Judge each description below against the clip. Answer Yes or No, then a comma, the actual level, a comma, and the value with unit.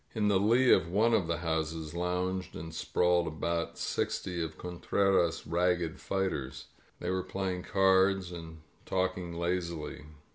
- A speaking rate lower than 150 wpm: Yes, average, 140 wpm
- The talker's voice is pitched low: Yes, very low, 90 Hz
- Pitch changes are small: Yes, narrow, 2.3 semitones